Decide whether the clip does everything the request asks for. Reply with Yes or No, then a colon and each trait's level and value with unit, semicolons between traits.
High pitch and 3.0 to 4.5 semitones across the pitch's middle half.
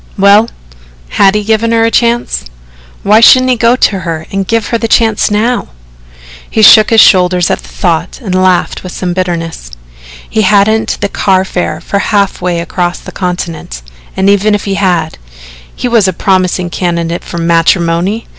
Yes: high, 195 Hz; average, 3.6 semitones